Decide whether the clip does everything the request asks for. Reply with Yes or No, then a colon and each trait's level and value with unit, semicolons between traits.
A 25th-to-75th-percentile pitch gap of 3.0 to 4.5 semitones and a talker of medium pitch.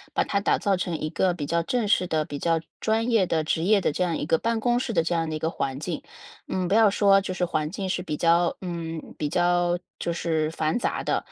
Yes: average, 3.4 semitones; medium, 175 Hz